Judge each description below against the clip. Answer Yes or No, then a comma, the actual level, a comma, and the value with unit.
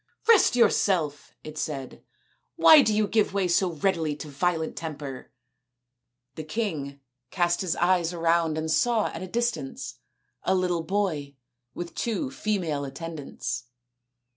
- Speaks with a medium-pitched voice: Yes, medium, 165 Hz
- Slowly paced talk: No, average, 145 wpm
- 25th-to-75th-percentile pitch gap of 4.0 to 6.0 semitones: Yes, average, 4.9 semitones